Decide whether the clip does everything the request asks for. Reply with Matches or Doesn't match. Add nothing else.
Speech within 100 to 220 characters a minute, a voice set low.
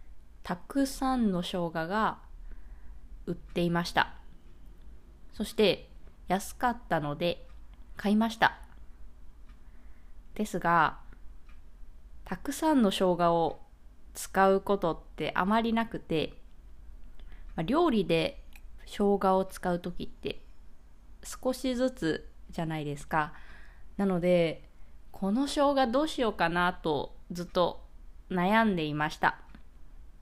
Doesn't match